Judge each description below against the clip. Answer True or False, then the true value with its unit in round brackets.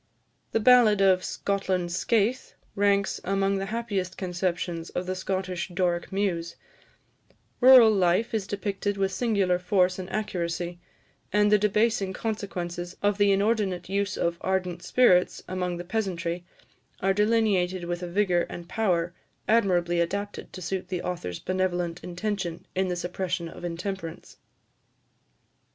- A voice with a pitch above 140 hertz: True (190 Hz)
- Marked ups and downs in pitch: False (2.5 semitones)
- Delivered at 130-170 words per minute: True (140 wpm)